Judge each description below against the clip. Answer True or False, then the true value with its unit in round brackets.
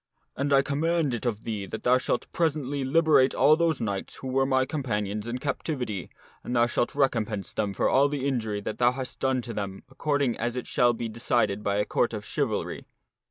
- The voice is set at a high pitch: False (125 Hz)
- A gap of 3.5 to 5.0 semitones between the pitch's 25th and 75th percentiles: True (4.2 semitones)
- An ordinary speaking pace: False (210 wpm)